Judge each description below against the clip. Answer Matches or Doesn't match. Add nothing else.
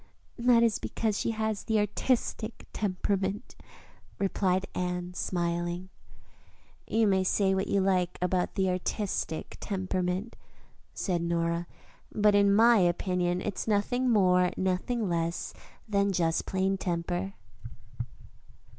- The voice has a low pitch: Doesn't match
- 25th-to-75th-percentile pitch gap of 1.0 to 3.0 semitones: Matches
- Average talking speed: Doesn't match